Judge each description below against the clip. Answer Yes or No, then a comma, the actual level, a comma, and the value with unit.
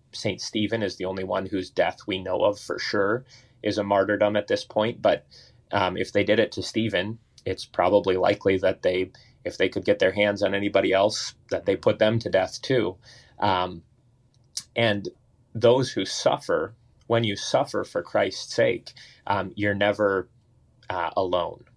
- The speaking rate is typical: Yes, average, 175 wpm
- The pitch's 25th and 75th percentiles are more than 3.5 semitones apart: No, average, 3.0 semitones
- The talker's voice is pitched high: No, low, 105 Hz